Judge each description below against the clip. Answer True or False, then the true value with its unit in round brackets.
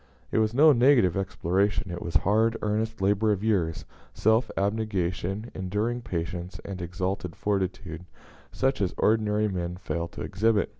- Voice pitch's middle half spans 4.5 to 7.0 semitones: False (3.4 semitones)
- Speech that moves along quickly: False (145 wpm)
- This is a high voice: False (100 Hz)